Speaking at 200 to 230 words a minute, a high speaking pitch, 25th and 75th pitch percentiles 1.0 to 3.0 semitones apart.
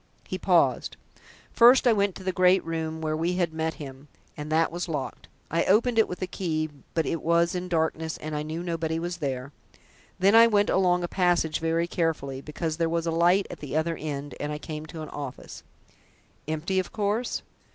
No: fast, 205 wpm; medium, 165 Hz; narrow, 2.6 semitones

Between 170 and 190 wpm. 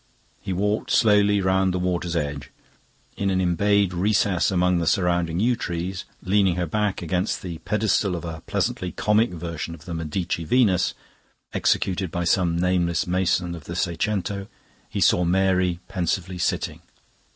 No: average, 150 wpm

